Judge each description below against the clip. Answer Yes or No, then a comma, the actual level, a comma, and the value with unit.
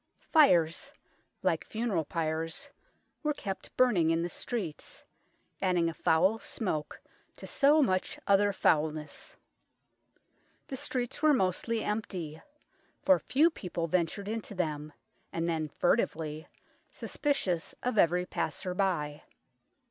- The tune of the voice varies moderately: No, wide, 5.7 semitones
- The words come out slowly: Yes, slow, 115 wpm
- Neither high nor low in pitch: Yes, medium, 180 Hz